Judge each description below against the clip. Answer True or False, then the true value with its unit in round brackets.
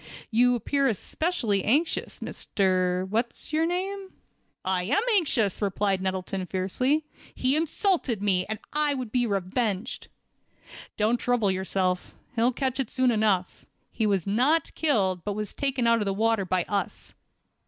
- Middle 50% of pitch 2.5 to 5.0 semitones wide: False (5.6 semitones)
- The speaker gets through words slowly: False (145 wpm)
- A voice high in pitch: True (220 Hz)